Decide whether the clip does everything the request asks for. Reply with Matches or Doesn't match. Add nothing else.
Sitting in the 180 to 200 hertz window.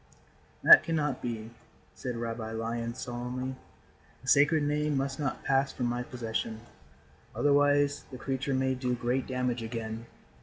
Doesn't match